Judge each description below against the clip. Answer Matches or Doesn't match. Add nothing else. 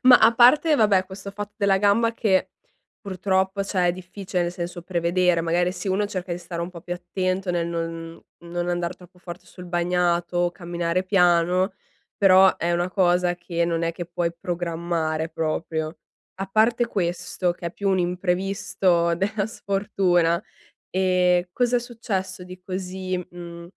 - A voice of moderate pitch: Matches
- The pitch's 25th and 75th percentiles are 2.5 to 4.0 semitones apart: Doesn't match